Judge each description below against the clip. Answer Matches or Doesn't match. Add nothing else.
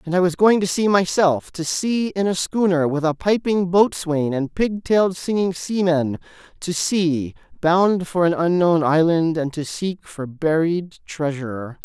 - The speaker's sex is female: Doesn't match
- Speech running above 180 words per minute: Doesn't match